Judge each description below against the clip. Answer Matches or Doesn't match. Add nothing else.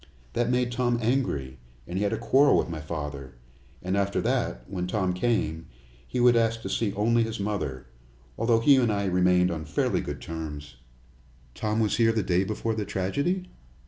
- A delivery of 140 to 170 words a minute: Doesn't match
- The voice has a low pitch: Matches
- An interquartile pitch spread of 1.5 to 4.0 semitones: Doesn't match